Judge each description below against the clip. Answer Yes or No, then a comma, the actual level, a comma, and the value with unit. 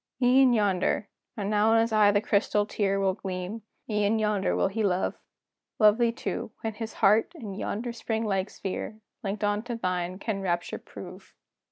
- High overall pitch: Yes, high, 210 Hz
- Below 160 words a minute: No, average, 180 wpm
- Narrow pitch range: Yes, narrow, 2.3 semitones